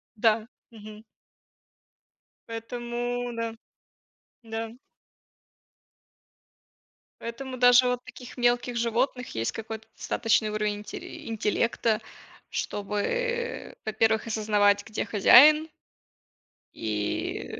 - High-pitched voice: Yes, high, 225 Hz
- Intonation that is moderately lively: No, narrow, 2.3 semitones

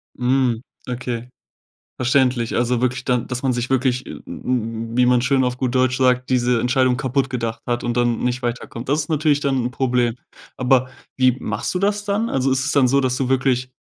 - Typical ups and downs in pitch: No, narrow, 1.4 semitones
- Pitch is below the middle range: Yes, low, 125 Hz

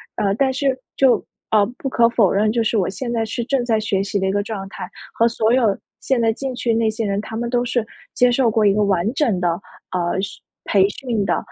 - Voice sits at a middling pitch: No, high, 225 Hz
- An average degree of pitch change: Yes, average, 3.3 semitones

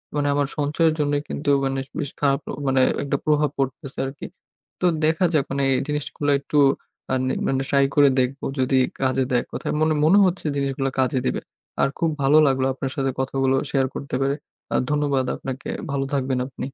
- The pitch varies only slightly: Yes, narrow, 1.6 semitones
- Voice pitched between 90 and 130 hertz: No, medium, 140 Hz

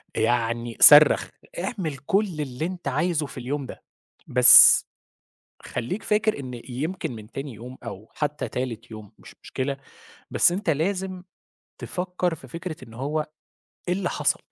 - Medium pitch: Yes, medium, 145 Hz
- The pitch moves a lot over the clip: Yes, wide, 6.3 semitones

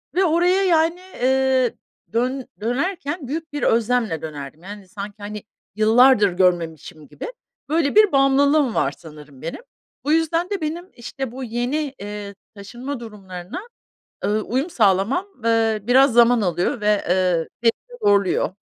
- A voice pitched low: No, high, 235 Hz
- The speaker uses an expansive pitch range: Yes, wide, 6.1 semitones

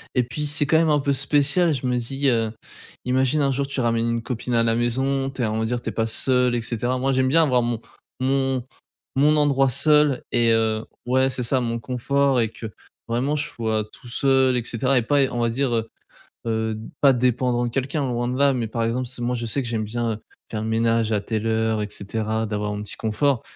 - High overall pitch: No, low, 125 Hz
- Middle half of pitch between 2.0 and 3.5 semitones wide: Yes, average, 3.0 semitones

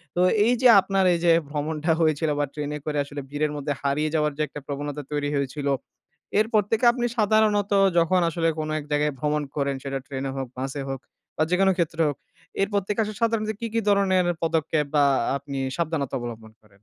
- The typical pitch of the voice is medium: Yes, medium, 150 Hz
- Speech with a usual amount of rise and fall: Yes, average, 4.9 semitones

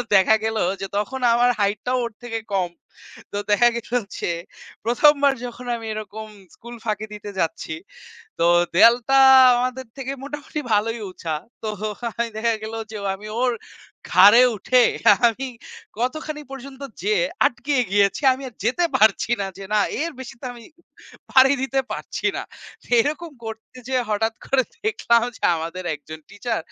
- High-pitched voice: Yes, high, 235 Hz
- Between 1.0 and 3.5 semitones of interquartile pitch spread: No, average, 3.9 semitones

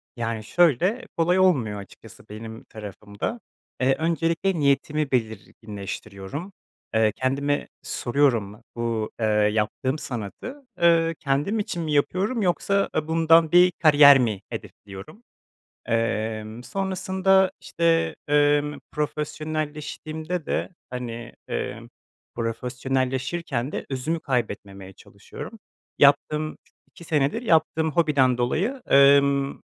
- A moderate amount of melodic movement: No, wide, 6.3 semitones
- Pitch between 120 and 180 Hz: Yes, medium, 140 Hz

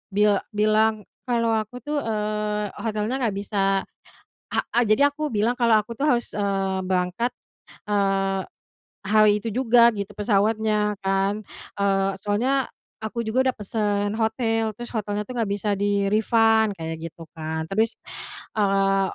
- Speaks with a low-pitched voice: No, high, 210 Hz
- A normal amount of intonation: No, narrow, 2.0 semitones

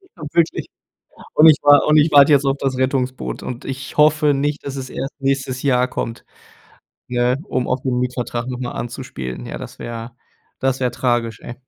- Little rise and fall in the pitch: Yes, narrow, 2.3 semitones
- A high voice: No, low, 130 Hz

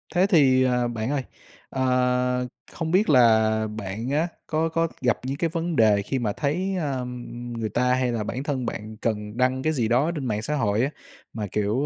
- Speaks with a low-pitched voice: Yes, low, 125 Hz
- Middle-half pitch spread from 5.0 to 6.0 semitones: No, average, 4.5 semitones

